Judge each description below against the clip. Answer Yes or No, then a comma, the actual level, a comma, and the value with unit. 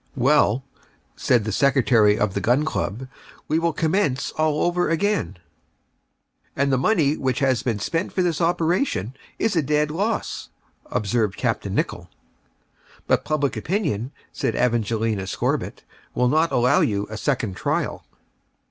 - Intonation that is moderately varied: No, wide, 6.1 semitones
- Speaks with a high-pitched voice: No, low, 135 Hz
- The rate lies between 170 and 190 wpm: No, average, 145 wpm